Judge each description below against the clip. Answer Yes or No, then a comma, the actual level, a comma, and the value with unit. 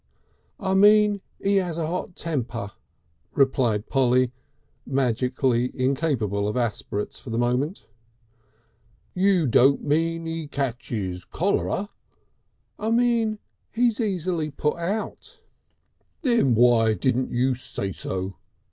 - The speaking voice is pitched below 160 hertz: Yes, medium, 140 Hz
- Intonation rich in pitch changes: Yes, wide, 7.3 semitones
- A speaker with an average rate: No, slow, 110 wpm